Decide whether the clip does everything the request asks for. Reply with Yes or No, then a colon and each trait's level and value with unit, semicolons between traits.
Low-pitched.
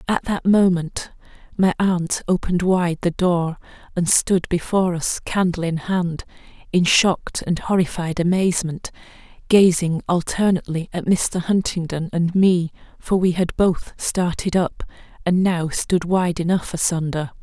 No: medium, 175 Hz